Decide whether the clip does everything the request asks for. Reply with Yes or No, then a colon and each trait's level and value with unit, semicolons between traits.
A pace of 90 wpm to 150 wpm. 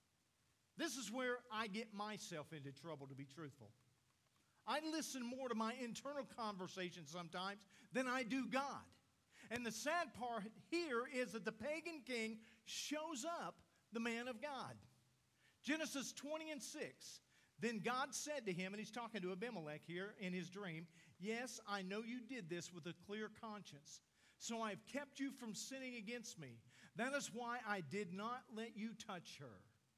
No: average, 170 wpm